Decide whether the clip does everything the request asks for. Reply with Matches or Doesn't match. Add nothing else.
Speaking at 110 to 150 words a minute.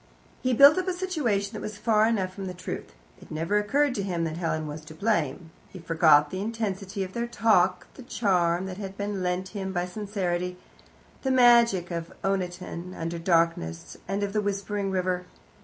Doesn't match